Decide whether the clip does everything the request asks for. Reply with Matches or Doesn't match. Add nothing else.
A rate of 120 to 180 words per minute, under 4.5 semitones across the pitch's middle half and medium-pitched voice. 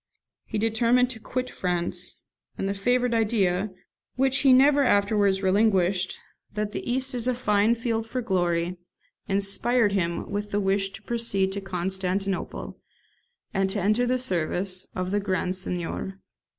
Doesn't match